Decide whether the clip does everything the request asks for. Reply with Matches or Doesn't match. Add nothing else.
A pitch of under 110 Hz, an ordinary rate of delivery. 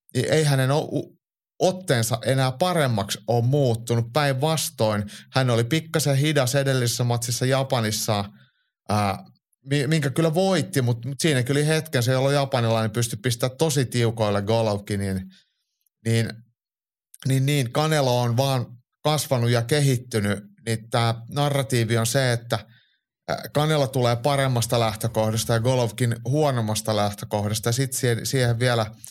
Doesn't match